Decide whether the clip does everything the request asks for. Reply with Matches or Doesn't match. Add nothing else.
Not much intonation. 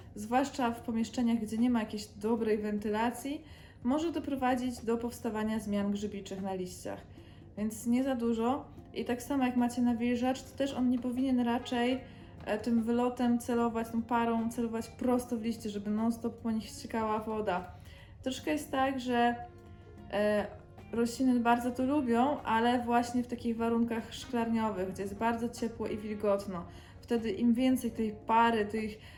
Matches